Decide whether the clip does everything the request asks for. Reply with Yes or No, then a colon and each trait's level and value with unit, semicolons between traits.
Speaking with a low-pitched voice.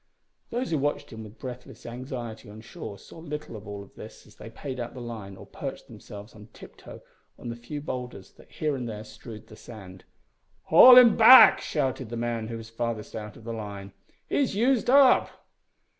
Yes: low, 120 Hz